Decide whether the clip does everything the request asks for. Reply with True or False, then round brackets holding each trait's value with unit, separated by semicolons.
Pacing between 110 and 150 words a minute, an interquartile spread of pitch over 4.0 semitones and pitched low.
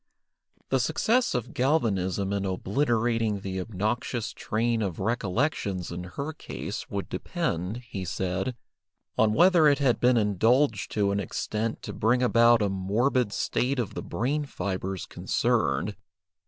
True (140 wpm; 4.5 semitones; 110 Hz)